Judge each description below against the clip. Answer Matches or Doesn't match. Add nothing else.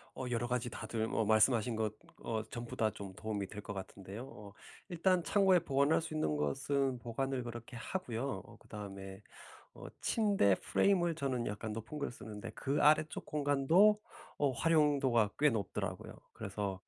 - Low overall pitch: Matches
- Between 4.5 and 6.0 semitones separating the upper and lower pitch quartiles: Matches